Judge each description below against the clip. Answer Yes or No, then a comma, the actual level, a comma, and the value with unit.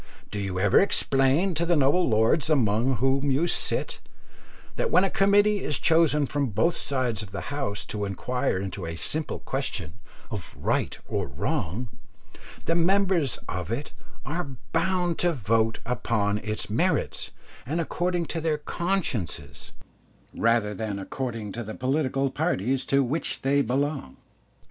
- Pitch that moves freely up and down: Yes, wide, 7.0 semitones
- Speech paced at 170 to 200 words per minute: No, average, 150 wpm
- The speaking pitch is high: No, low, 135 Hz